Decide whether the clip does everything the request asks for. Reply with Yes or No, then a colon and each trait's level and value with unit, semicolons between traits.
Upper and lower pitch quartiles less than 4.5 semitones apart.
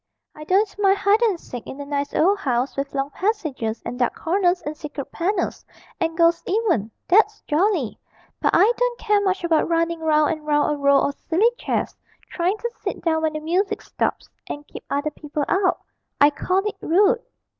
No: average, 5.2 semitones